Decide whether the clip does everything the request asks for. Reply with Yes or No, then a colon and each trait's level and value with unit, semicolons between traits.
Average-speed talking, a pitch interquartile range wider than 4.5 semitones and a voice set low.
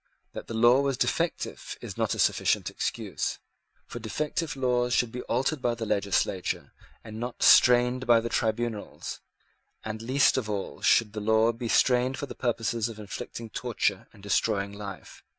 No: average, 170 wpm; narrow, 2.4 semitones; low, 115 Hz